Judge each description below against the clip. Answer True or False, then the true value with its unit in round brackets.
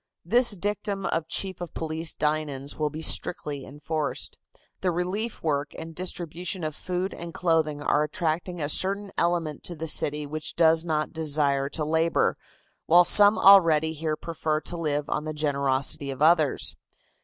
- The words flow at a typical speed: True (160 wpm)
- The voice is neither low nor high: True (160 Hz)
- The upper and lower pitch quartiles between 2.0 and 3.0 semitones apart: True (2.7 semitones)